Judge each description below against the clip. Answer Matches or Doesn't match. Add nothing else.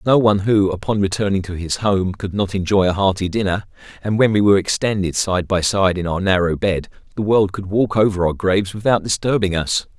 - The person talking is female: Doesn't match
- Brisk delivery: Matches